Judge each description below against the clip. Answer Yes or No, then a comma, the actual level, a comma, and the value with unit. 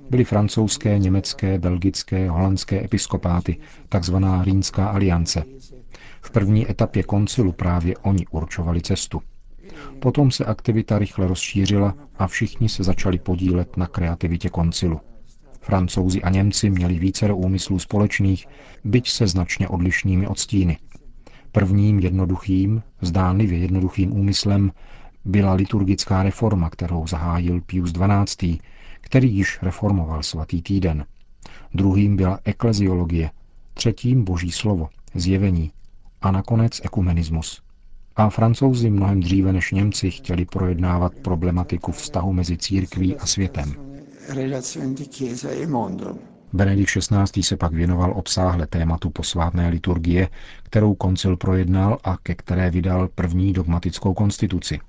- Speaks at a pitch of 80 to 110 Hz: Yes, very low, 95 Hz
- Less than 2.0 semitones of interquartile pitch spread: No, narrow, 2.4 semitones